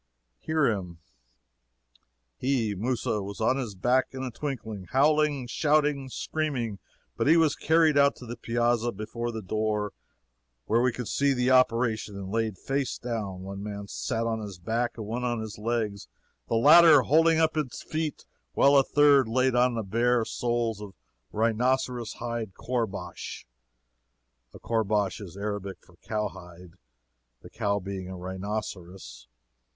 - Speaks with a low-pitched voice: Yes, low, 115 Hz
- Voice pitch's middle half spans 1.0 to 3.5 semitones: No, average, 4.2 semitones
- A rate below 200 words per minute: Yes, average, 150 wpm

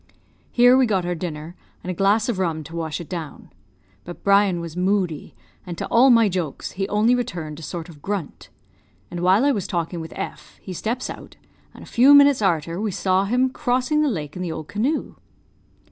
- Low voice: No, medium, 185 Hz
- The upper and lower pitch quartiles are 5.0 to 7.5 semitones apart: Yes, wide, 5.4 semitones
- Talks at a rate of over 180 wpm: Yes, fast, 205 wpm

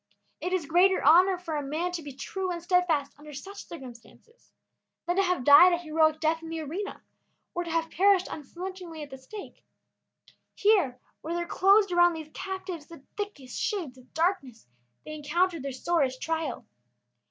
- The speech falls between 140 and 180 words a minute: Yes, average, 175 wpm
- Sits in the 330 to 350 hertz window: Yes, very high, 335 Hz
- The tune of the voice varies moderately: Yes, average, 3.7 semitones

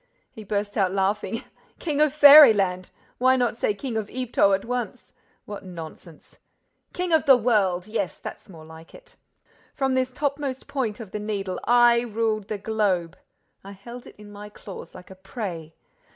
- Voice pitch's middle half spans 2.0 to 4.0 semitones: No, average, 4.4 semitones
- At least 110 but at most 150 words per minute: No, average, 170 wpm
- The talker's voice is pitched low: No, high, 215 Hz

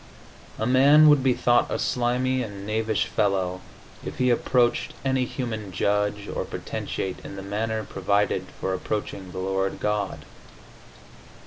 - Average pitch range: Yes, average, 4.1 semitones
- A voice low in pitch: Yes, low, 105 Hz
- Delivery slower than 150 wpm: Yes, average, 140 wpm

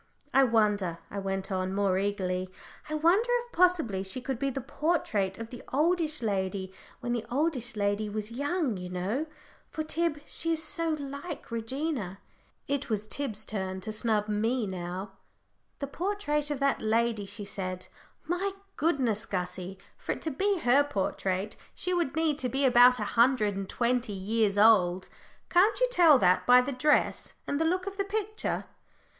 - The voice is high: Yes, high, 240 Hz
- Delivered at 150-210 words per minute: Yes, average, 175 wpm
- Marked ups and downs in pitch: Yes, wide, 7.1 semitones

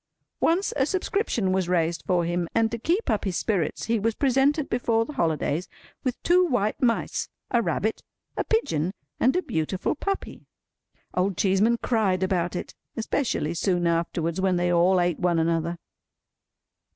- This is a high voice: Yes, high, 195 Hz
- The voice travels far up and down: Yes, wide, 5.9 semitones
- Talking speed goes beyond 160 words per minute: No, average, 155 wpm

